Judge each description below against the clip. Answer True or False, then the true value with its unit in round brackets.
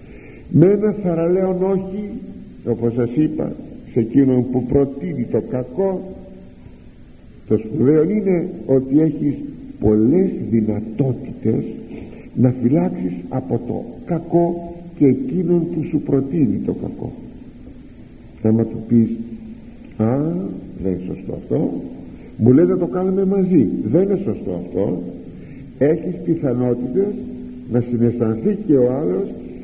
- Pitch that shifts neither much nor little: False (7.5 semitones)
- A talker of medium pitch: True (145 Hz)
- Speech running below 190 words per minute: True (115 wpm)